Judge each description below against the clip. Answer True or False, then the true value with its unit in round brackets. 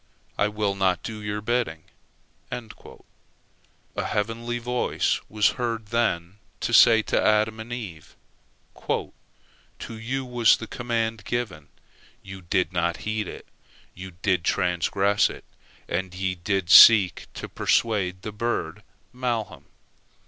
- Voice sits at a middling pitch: False (105 Hz)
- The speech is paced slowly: True (125 wpm)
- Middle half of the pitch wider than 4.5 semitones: False (3.7 semitones)